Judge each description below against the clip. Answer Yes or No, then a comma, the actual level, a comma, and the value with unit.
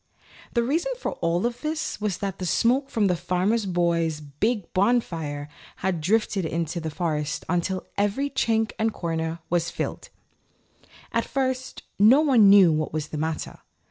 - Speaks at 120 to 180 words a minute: Yes, average, 155 wpm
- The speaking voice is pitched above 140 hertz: Yes, high, 190 Hz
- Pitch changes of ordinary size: No, wide, 6.0 semitones